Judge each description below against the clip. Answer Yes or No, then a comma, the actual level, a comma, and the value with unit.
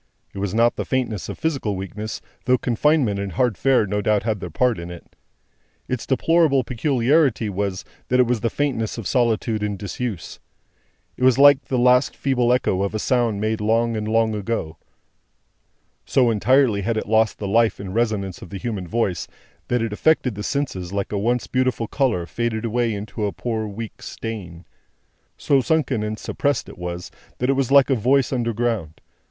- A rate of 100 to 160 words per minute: No, average, 185 wpm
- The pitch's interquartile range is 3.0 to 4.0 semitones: Yes, average, 3.6 semitones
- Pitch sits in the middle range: No, low, 115 Hz